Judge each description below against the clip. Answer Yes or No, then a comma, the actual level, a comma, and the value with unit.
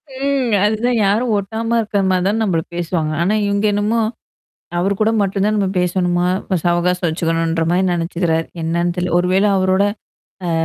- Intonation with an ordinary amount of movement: Yes, average, 3.3 semitones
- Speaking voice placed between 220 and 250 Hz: No, medium, 185 Hz